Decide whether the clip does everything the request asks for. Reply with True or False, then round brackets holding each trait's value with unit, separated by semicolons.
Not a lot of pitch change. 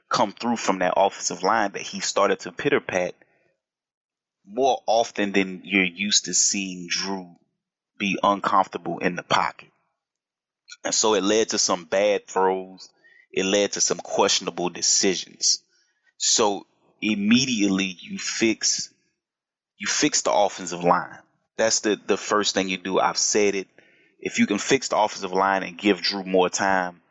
True (1.8 semitones)